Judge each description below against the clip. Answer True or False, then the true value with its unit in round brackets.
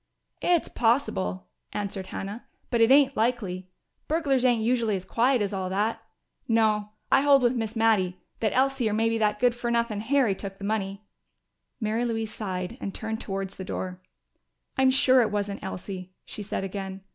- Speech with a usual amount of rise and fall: True (3.7 semitones)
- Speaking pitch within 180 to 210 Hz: False (220 Hz)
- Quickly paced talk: False (175 wpm)